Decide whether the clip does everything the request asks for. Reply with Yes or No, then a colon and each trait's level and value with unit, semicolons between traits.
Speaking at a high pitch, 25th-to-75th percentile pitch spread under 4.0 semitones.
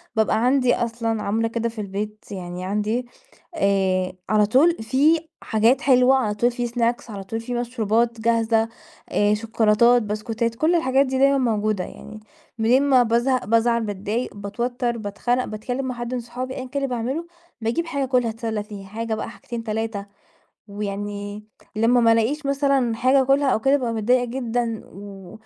Yes: high, 230 Hz; average, 3.0 semitones